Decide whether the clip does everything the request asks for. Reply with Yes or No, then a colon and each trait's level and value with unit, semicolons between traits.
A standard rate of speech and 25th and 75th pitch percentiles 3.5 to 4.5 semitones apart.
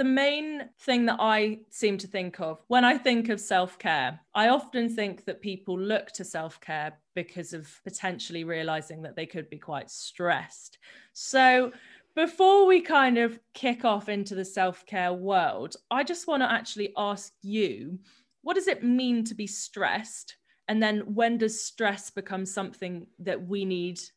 No: average, 175 wpm; average, 4.9 semitones